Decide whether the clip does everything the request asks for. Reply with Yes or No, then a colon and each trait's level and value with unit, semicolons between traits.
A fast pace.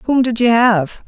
Yes: fast, 225 wpm